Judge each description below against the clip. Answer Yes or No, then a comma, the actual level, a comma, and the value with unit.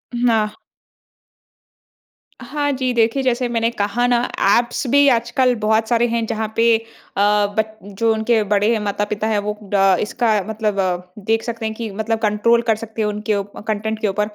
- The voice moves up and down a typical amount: No, narrow, 2.0 semitones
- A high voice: Yes, high, 220 Hz